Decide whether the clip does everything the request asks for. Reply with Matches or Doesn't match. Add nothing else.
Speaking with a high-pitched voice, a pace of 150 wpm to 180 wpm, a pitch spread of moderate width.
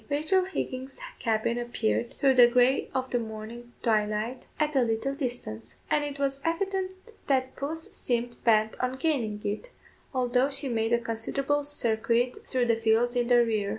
Matches